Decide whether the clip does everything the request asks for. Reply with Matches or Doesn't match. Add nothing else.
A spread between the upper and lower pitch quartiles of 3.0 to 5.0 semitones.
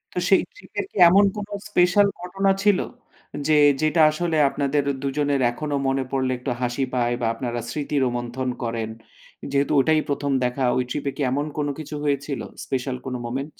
Matches